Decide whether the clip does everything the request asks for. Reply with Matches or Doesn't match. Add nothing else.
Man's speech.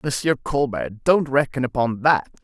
Matches